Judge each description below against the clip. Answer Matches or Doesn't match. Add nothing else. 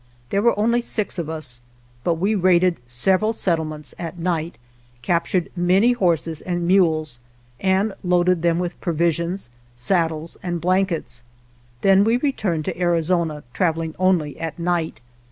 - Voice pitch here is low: Doesn't match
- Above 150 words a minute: Doesn't match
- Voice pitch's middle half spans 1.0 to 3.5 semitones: Matches